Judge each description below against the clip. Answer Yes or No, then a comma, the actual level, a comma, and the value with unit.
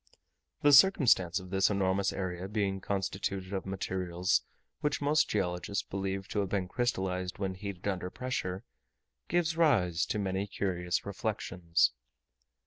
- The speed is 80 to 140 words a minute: Yes, slow, 135 wpm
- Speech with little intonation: Yes, narrow, 2.0 semitones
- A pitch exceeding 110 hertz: No, very low, 95 Hz